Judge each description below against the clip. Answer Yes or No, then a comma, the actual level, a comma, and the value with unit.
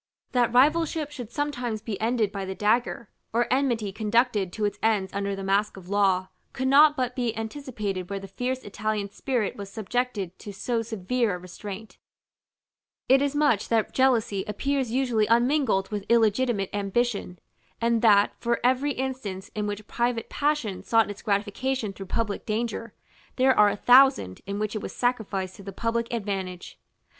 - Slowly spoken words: No, average, 170 wpm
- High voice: Yes, high, 220 Hz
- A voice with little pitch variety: No, average, 3.7 semitones